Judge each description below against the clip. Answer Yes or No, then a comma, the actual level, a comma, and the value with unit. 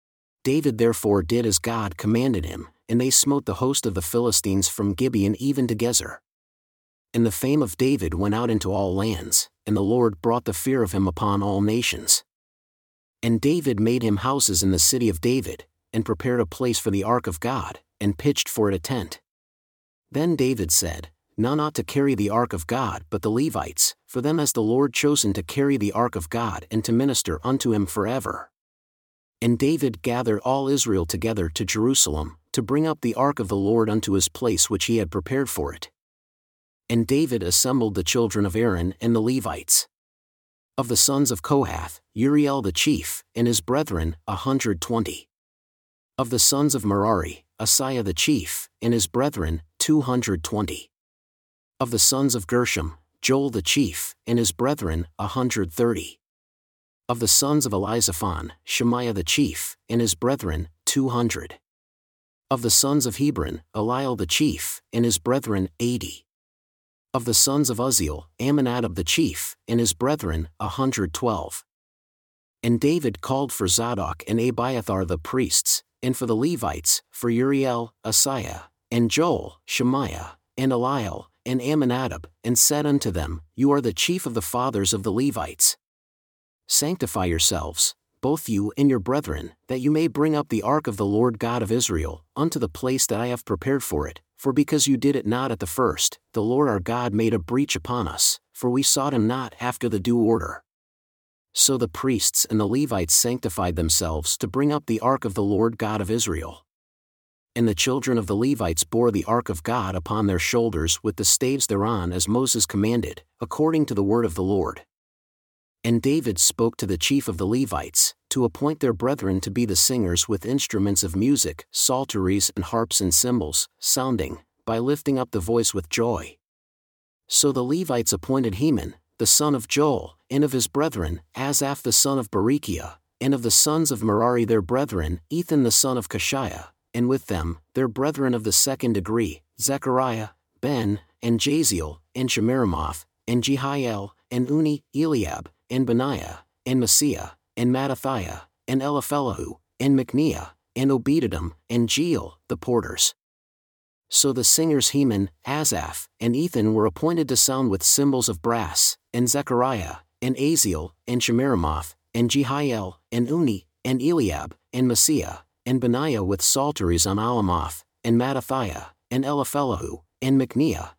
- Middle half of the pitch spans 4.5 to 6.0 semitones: Yes, wide, 5.4 semitones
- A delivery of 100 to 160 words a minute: No, average, 175 wpm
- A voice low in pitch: Yes, low, 115 Hz